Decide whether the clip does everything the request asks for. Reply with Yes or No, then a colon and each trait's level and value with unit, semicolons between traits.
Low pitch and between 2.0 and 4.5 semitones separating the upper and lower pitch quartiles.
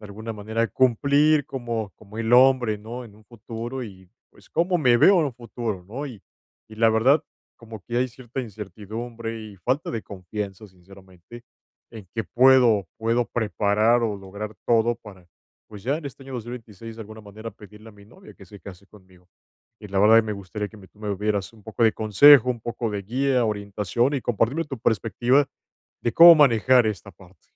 Yes: low, 110 Hz; average, 2.9 semitones